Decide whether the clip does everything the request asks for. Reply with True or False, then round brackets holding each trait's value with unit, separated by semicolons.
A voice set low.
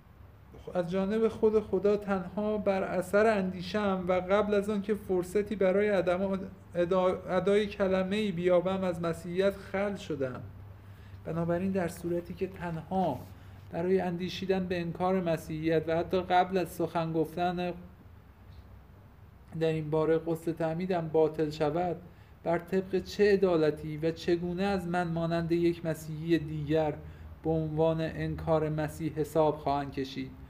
False (175 Hz)